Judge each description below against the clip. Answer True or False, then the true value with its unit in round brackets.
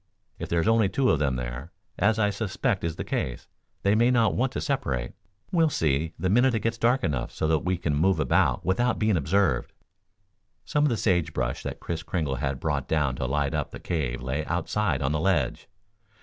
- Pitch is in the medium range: False (85 Hz)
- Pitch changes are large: True (7.4 semitones)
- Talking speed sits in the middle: False (210 wpm)